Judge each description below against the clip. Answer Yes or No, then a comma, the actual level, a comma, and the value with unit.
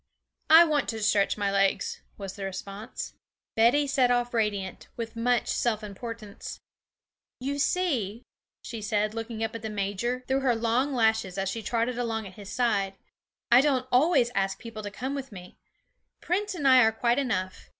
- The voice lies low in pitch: No, high, 230 Hz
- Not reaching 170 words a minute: No, average, 175 wpm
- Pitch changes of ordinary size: Yes, average, 3.7 semitones